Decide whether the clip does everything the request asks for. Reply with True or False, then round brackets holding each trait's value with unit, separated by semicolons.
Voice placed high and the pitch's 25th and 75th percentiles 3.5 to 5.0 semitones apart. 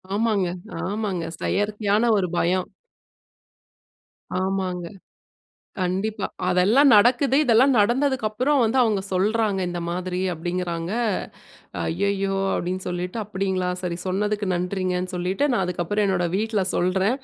False (195 Hz; 3.0 semitones)